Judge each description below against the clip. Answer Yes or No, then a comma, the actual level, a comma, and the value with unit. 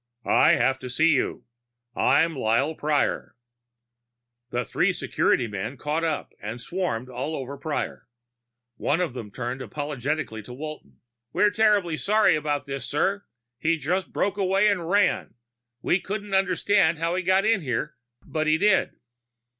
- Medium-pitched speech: Yes, medium, 155 Hz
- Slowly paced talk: No, average, 150 wpm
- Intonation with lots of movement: Yes, wide, 5.9 semitones